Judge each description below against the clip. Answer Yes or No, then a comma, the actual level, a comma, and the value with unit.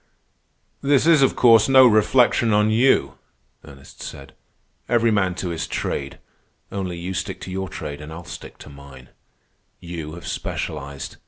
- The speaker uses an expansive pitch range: Yes, wide, 6.9 semitones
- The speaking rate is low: No, average, 155 wpm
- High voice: No, very low, 90 Hz